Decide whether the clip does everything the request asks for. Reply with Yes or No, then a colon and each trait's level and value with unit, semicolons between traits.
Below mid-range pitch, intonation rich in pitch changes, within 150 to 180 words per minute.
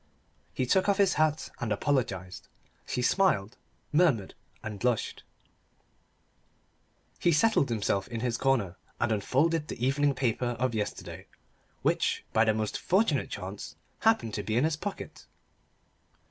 No: low, 125 Hz; wide, 6.1 semitones; slow, 135 wpm